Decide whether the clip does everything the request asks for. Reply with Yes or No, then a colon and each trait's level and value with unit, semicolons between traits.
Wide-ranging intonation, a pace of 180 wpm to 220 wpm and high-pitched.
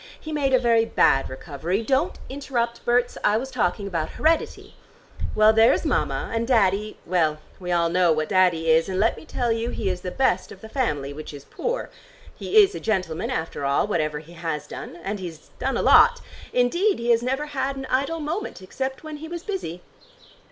Yes: wide, 7.7 semitones; average, 200 wpm; high, 225 Hz